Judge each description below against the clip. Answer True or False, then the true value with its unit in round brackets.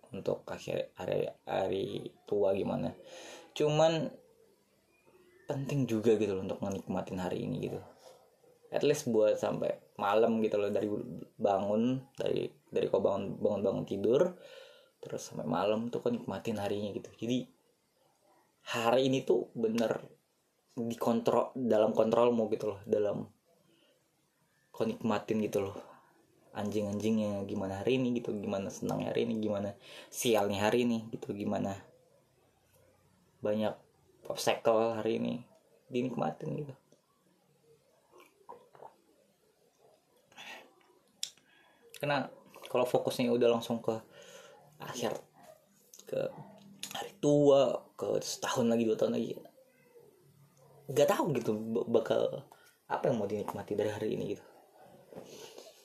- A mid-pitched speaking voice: False (130 Hz)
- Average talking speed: True (115 wpm)